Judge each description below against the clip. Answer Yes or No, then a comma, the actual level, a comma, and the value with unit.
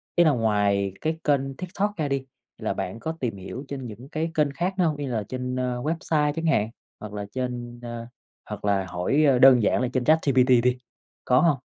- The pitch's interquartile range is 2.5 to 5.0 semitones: Yes, average, 4.5 semitones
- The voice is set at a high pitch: No, low, 130 Hz